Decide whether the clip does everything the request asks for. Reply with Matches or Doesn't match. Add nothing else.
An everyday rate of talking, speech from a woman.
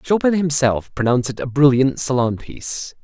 Doesn't match